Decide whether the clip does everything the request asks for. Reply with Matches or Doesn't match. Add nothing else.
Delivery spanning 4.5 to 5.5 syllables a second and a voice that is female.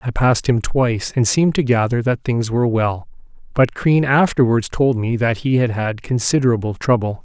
Doesn't match